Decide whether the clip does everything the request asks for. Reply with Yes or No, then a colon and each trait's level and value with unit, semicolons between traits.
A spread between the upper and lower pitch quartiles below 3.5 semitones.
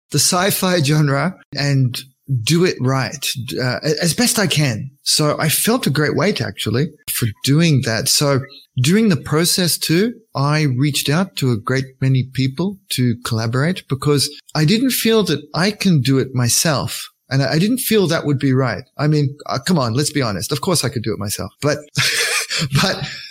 No: average, 4.6 semitones